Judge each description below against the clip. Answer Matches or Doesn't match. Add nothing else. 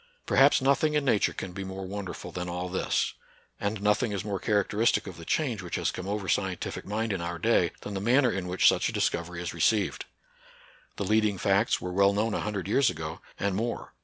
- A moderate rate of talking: Doesn't match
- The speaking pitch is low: Matches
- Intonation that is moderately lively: Matches